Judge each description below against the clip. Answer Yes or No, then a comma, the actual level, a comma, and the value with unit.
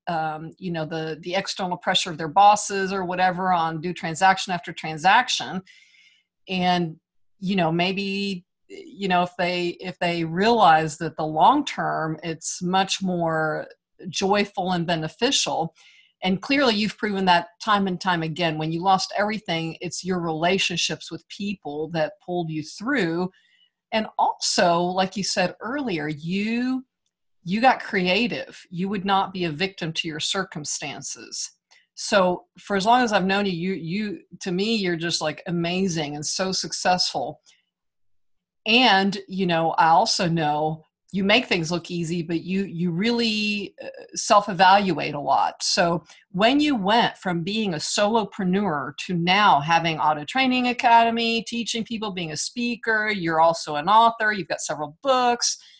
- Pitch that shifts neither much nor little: Yes, average, 3.8 semitones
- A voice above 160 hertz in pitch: Yes, medium, 185 Hz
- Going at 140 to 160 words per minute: Yes, average, 155 wpm